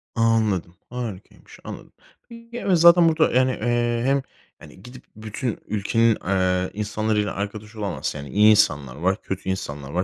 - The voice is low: Yes, low, 105 Hz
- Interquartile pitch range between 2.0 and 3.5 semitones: No, average, 4.2 semitones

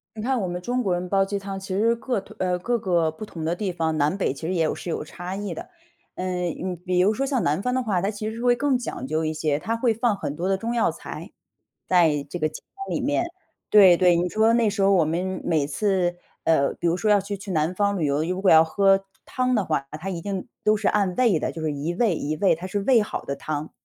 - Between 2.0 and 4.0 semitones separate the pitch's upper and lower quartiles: No, average, 4.4 semitones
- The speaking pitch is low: No, high, 190 Hz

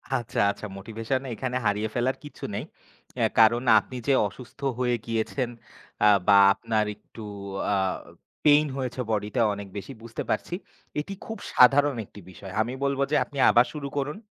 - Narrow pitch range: No, average, 4.0 semitones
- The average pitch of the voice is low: Yes, low, 120 Hz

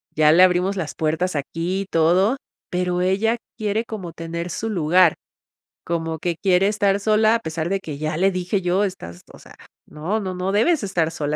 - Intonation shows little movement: No, average, 3.4 semitones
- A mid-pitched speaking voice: Yes, medium, 180 Hz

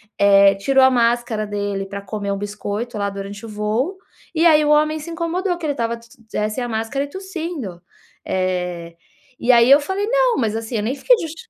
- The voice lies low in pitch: No, high, 235 Hz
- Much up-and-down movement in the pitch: Yes, wide, 7.0 semitones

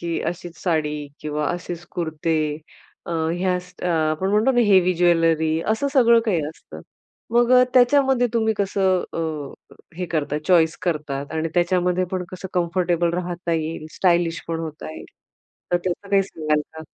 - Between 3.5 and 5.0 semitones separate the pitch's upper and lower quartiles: No, average, 2.8 semitones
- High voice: No, medium, 175 Hz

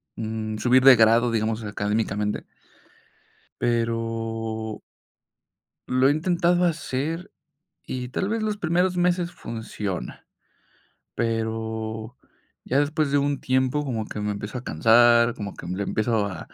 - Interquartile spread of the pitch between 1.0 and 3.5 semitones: No, average, 4.5 semitones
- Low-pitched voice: Yes, low, 115 Hz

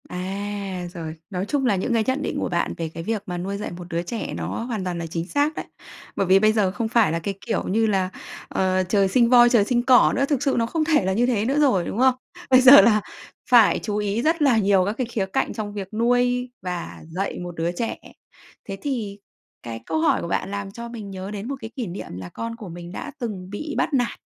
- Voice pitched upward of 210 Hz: No, high, 205 Hz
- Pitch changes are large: No, average, 4.6 semitones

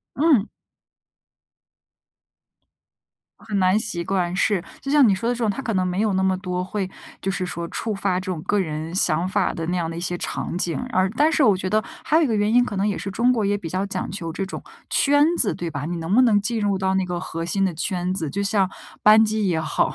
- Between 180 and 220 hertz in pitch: Yes, high, 195 Hz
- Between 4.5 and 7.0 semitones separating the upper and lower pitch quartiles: No, average, 3.1 semitones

